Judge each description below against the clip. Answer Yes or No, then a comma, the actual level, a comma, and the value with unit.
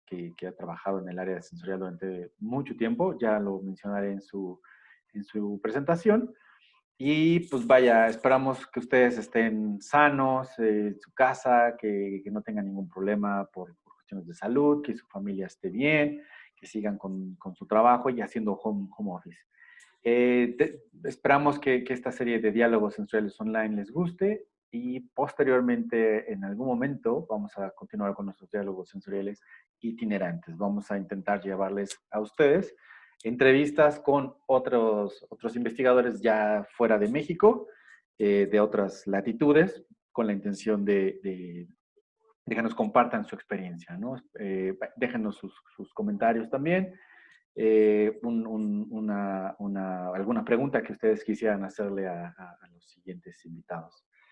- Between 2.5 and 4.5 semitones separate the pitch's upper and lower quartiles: No, average, 5.1 semitones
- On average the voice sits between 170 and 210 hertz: No, low, 110 Hz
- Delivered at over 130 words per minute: Yes, average, 150 wpm